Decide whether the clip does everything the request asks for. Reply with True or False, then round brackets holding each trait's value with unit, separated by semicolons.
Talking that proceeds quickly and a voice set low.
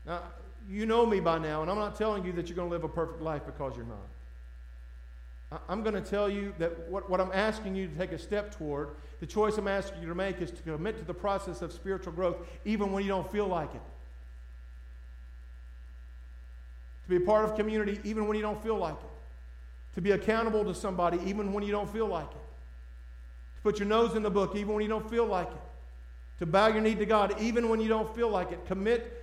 False (235 wpm; 185 Hz)